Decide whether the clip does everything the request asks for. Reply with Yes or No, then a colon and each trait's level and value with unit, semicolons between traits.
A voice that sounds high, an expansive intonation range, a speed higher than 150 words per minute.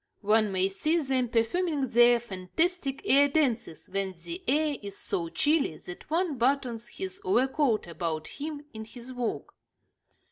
No: high, 245 Hz; wide, 6.7 semitones; average, 145 wpm